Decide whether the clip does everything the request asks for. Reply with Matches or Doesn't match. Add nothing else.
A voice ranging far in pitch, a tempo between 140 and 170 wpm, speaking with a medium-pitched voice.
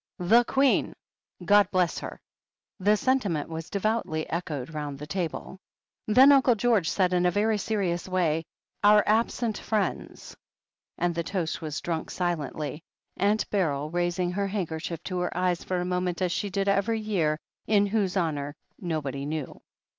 Doesn't match